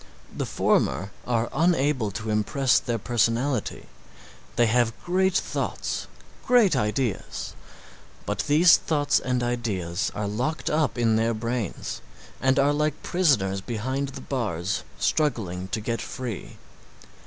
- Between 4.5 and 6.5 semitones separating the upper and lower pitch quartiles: Yes, average, 4.9 semitones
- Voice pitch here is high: No, low, 120 Hz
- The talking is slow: Yes, slow, 125 wpm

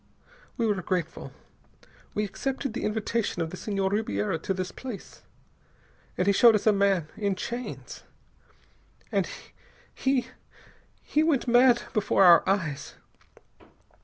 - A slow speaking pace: Yes, slow, 125 wpm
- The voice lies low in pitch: No, high, 205 Hz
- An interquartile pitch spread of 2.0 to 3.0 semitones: No, average, 4.4 semitones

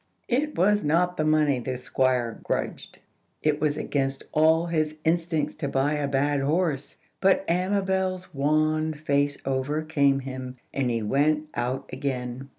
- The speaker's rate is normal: Yes, average, 145 wpm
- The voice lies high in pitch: No, medium, 150 Hz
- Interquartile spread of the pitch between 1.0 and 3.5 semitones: Yes, average, 3.1 semitones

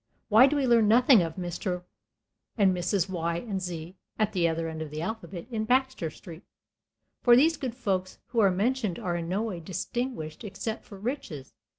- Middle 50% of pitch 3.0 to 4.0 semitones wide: No, wide, 5.4 semitones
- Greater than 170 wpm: Yes, average, 190 wpm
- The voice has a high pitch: Yes, high, 195 Hz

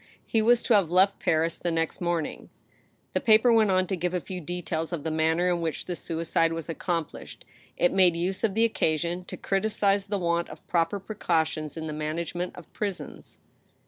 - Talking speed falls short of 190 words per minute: No, fast, 205 wpm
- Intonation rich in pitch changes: No, average, 3.0 semitones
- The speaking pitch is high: No, medium, 175 Hz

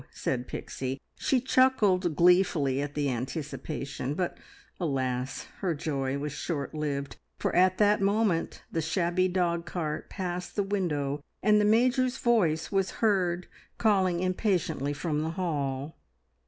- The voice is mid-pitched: Yes, medium, 170 Hz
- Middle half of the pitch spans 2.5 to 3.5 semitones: No, average, 5.1 semitones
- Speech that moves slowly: Yes, slow, 130 wpm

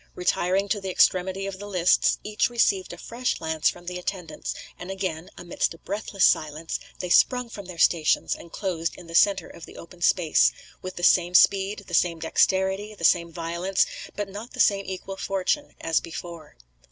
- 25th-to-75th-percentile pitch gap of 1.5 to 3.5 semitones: Yes, narrow, 2.5 semitones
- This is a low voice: No, medium, 185 Hz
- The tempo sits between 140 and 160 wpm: No, average, 190 wpm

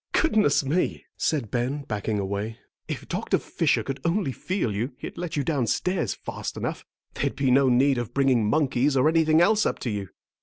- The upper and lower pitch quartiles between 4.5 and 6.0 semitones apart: Yes, average, 5.0 semitones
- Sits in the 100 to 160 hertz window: Yes, low, 135 Hz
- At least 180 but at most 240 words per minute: Yes, average, 185 wpm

